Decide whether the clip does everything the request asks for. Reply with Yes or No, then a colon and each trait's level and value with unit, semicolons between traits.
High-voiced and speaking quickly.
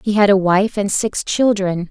Yes: high, 200 Hz; fast, 220 wpm